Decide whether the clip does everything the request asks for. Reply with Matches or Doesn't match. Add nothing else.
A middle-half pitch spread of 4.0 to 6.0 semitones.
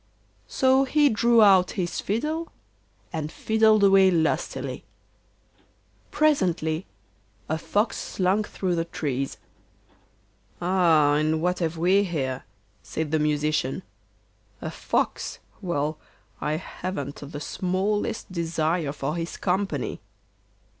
Matches